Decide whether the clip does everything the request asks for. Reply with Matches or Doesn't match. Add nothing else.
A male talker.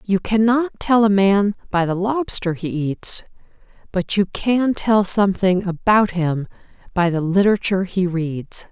Doesn't match